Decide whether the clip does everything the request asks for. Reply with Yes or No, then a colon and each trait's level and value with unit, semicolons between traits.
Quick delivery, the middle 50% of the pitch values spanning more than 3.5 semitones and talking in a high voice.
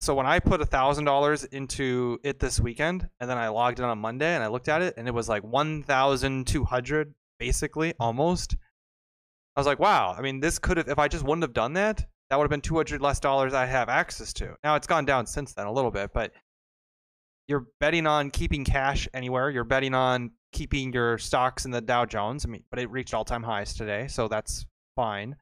No: fast, 220 wpm; average, 3.9 semitones; low, 130 Hz